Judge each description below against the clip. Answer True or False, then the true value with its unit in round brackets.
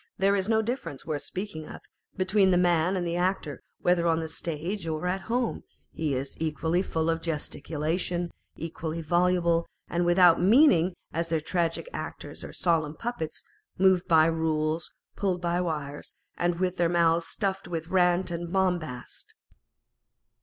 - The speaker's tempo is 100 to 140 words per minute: False (160 wpm)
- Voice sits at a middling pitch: True (170 Hz)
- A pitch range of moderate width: False (2.3 semitones)